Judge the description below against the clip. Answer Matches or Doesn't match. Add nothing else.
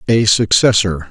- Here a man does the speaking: Matches